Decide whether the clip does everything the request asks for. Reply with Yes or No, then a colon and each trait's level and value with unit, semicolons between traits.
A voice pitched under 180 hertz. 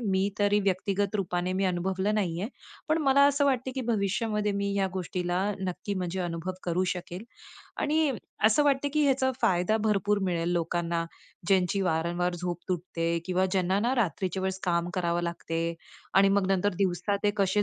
No: high, 190 Hz